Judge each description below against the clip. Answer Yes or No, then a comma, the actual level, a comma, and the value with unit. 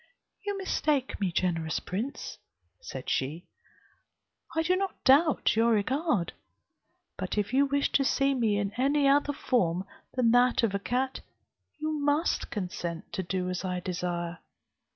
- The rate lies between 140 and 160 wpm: Yes, average, 150 wpm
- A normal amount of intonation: No, wide, 7.6 semitones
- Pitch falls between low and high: No, high, 240 Hz